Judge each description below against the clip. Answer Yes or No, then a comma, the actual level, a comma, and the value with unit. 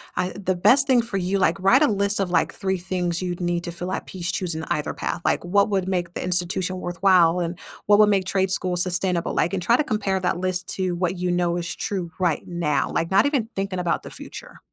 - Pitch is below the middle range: No, medium, 185 Hz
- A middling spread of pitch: No, narrow, 1.9 semitones